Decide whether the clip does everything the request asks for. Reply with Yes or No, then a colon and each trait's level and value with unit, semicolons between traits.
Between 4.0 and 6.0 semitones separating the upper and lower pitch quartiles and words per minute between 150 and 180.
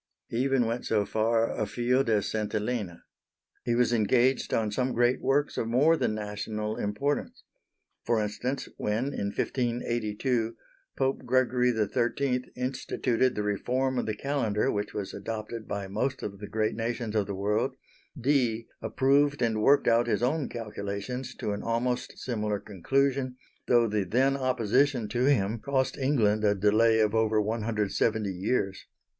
No: average, 3.2 semitones; average, 160 wpm